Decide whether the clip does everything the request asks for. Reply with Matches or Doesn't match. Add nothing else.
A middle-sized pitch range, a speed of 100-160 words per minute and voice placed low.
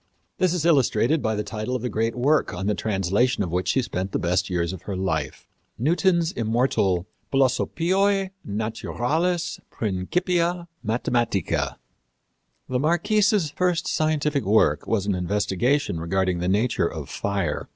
Doesn't match